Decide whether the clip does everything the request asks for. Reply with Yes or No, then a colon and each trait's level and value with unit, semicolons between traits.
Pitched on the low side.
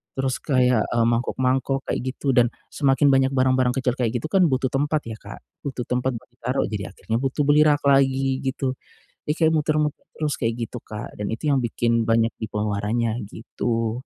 Yes: low, 130 Hz